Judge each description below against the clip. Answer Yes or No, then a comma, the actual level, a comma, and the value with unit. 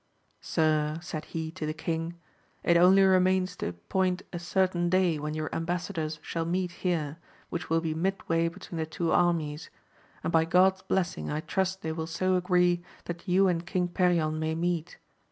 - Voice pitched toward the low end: No, medium, 170 Hz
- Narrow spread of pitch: Yes, narrow, 2.3 semitones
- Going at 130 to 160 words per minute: No, average, 180 wpm